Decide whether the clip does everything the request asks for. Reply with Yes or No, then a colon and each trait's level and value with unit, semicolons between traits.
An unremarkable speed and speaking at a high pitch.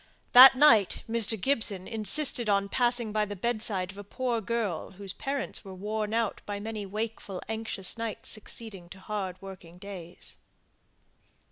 Yes: average, 150 wpm; high, 210 Hz